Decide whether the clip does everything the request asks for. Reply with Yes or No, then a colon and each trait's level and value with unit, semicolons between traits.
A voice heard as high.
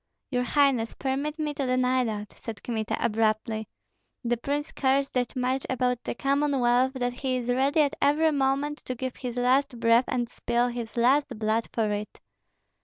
Yes: very high, 250 Hz